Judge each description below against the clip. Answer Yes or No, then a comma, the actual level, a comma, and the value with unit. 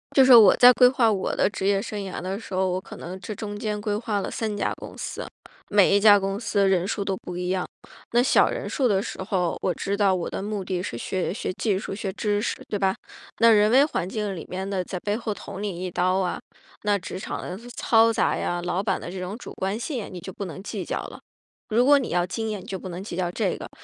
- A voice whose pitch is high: Yes, high, 200 Hz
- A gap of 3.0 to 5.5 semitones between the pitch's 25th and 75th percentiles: No, narrow, 2.5 semitones